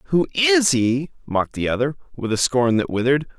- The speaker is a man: Yes, male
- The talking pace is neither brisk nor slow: Yes, average, 195 wpm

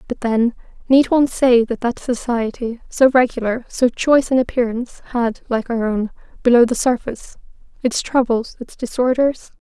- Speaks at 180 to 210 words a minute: No, average, 155 wpm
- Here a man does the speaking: No, female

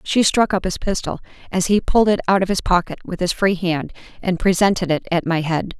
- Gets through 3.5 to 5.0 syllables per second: No, 5.7 syllables/s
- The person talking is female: Yes, female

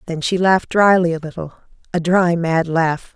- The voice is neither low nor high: Yes, medium, 170 Hz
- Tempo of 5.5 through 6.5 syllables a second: No, 4.8 syllables/s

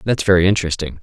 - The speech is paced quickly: No, average, 175 wpm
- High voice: No, very low, 90 Hz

